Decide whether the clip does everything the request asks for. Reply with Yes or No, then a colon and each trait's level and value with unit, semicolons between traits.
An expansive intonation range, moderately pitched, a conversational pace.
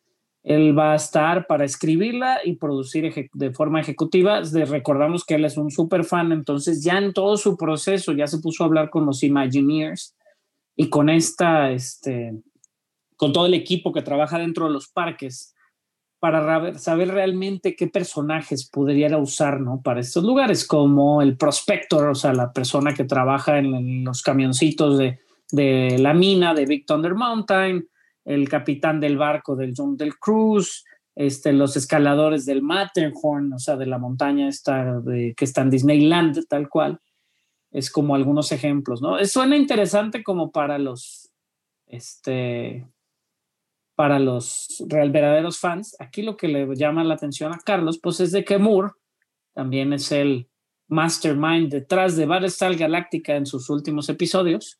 No: average, 3.6 semitones; medium, 150 Hz; average, 160 wpm